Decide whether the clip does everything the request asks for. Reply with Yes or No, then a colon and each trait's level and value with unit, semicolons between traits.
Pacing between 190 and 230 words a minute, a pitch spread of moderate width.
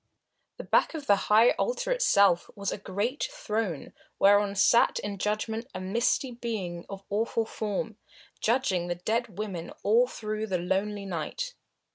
No: average, 150 wpm; average, 3.2 semitones